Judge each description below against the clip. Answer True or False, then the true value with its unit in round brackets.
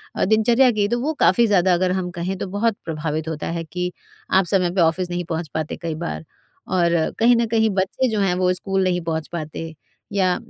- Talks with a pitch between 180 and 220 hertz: True (185 Hz)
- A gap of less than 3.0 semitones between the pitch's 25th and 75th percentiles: False (3.6 semitones)